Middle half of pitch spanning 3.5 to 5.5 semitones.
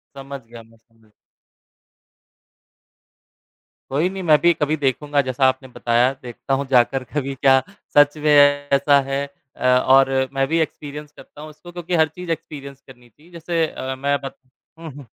No: narrow, 2.6 semitones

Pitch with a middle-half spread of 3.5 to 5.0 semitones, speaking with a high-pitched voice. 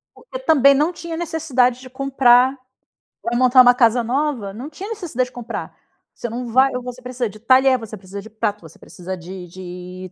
Yes: average, 4.1 semitones; very high, 250 Hz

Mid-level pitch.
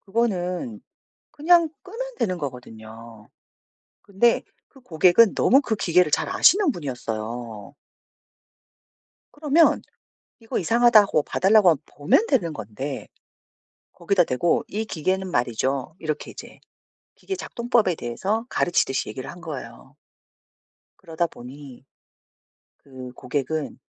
Yes: medium, 170 Hz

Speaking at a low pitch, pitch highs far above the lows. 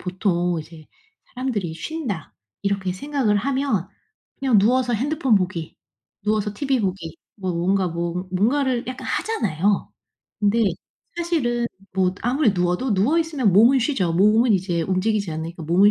No: high, 205 Hz; wide, 5.8 semitones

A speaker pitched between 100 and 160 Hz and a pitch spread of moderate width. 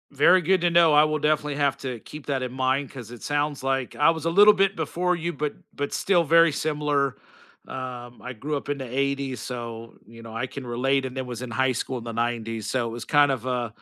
Yes: low, 135 Hz; average, 3.4 semitones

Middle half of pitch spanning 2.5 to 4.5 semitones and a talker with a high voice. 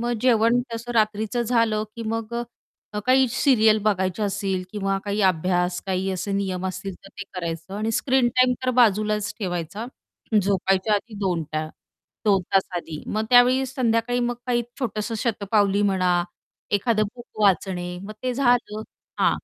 Yes: average, 3.7 semitones; high, 210 Hz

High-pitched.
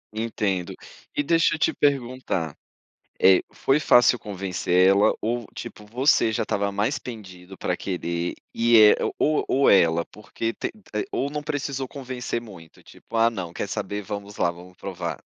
No: low, 105 Hz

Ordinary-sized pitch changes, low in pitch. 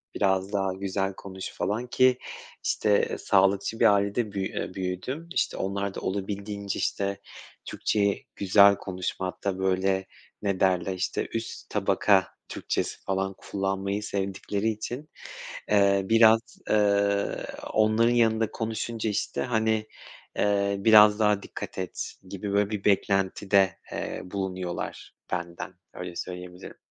No: narrow, 1.8 semitones; low, 100 Hz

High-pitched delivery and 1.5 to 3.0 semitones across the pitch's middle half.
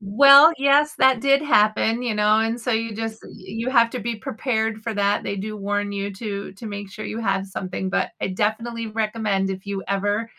Yes: high, 215 Hz; narrow, 2.4 semitones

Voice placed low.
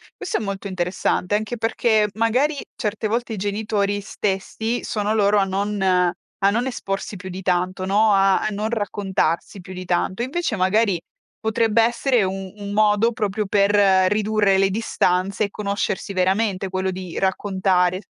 No: high, 200 Hz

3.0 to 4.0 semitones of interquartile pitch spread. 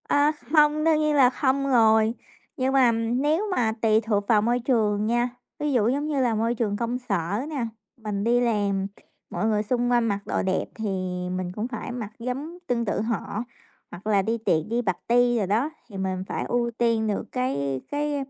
Yes: average, 3.5 semitones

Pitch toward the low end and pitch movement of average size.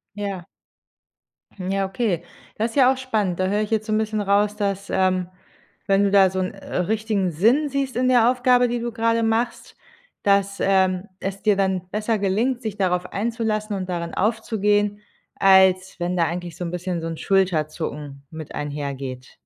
No: high, 200 Hz; average, 3.3 semitones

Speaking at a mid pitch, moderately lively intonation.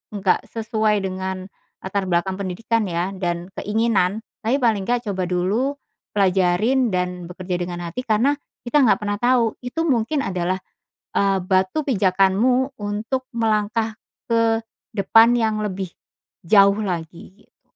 No: high, 205 Hz; average, 3.6 semitones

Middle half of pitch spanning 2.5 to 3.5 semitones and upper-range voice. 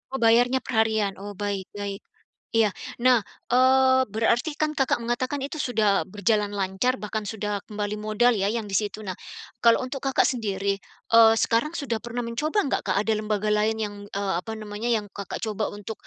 Yes: average, 2.9 semitones; high, 220 Hz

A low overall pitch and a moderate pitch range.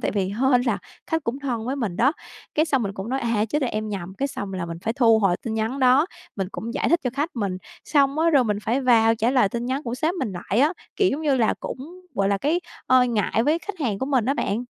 No: high, 245 Hz; average, 4.5 semitones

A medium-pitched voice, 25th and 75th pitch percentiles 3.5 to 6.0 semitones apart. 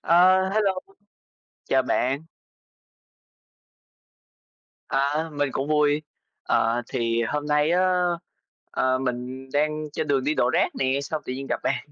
No: medium, 145 Hz; average, 2.9 semitones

